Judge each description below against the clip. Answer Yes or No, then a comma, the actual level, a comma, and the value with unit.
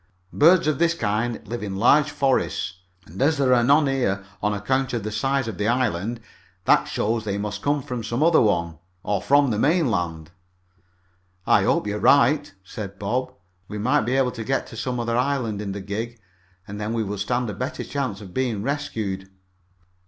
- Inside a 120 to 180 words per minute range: No, average, 195 wpm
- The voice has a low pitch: Yes, low, 115 Hz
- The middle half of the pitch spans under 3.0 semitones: No, average, 4.7 semitones